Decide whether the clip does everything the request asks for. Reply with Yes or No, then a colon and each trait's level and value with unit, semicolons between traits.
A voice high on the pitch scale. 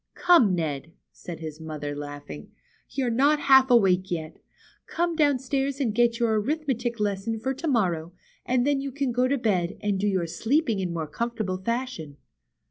Yes: high, 225 Hz